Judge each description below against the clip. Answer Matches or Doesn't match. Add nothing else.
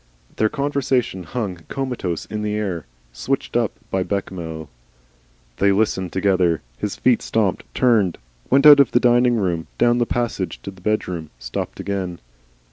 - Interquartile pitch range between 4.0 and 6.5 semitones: Matches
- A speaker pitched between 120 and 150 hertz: Doesn't match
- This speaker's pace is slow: Doesn't match